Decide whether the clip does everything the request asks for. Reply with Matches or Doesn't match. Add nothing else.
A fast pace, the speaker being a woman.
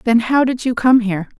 Matches